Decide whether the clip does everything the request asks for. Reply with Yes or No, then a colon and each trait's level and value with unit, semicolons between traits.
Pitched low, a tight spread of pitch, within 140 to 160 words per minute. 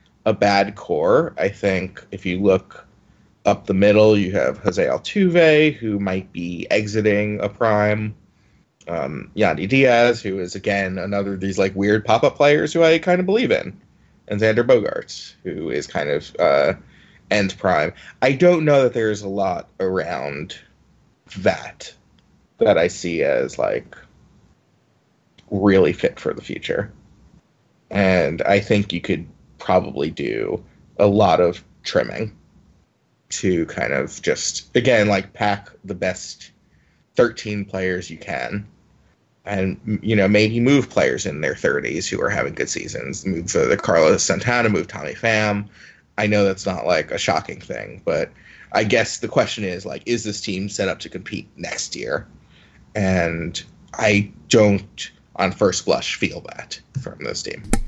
Yes: low, 100 Hz; narrow, 2.3 semitones; average, 155 wpm